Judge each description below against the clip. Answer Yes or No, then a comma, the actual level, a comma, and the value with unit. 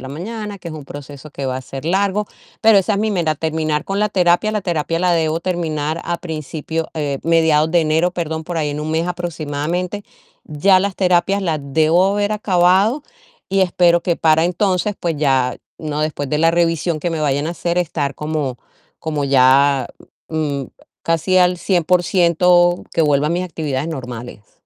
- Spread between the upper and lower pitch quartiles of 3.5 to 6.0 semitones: No, average, 3.1 semitones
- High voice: No, medium, 165 Hz